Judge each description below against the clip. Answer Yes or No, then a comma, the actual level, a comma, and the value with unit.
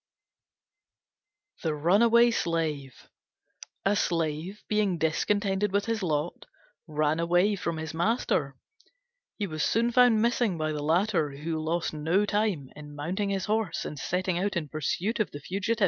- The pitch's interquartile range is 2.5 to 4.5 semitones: No, average, 4.9 semitones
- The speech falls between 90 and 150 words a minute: Yes, average, 145 wpm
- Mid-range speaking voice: Yes, medium, 175 Hz